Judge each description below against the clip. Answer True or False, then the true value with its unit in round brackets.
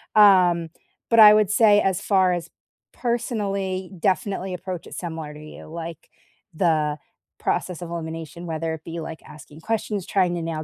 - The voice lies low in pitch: False (175 Hz)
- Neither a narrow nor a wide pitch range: True (3.3 semitones)